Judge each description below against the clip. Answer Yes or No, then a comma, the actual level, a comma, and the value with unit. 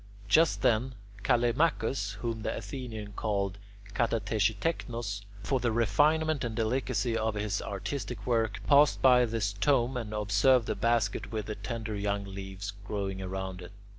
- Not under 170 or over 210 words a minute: No, average, 145 wpm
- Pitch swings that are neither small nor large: Yes, average, 3.4 semitones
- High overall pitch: No, low, 110 Hz